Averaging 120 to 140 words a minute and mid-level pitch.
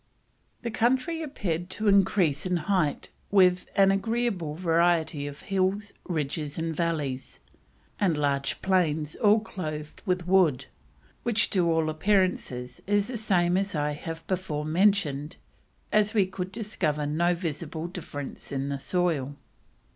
Yes: slow, 135 wpm; medium, 175 Hz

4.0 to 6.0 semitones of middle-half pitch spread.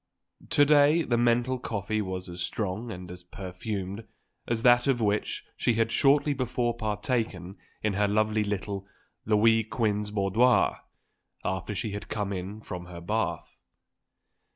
No: average, 3.4 semitones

